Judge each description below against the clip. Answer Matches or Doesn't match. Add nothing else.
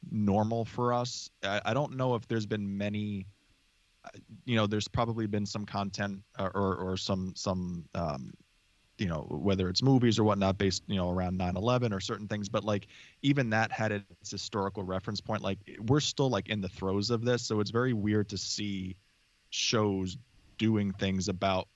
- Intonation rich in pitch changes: Doesn't match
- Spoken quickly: Doesn't match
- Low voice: Matches